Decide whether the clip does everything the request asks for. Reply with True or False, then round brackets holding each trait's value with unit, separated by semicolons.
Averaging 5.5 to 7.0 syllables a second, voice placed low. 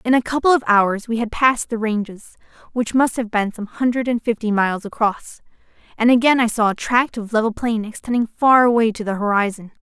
False (5.6 syllables/s; 225 Hz)